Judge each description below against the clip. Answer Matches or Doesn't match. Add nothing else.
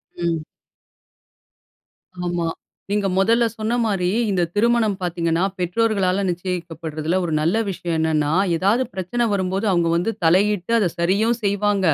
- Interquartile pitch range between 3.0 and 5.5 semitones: Matches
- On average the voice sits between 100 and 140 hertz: Doesn't match